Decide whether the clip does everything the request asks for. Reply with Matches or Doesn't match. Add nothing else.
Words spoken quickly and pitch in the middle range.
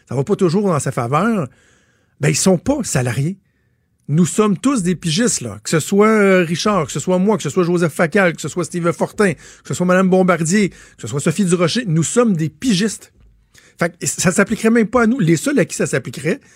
Matches